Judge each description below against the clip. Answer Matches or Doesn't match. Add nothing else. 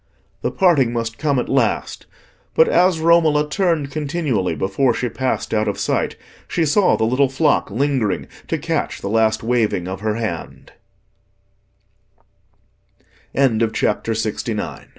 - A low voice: Matches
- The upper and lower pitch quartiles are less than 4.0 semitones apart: Doesn't match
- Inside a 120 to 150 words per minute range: Matches